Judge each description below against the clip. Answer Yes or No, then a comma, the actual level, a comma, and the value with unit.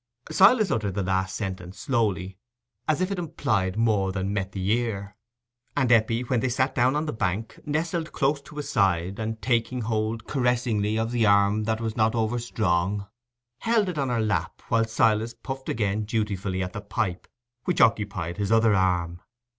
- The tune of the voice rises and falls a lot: No, average, 3.8 semitones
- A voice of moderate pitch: No, low, 110 Hz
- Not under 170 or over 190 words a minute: Yes, average, 180 wpm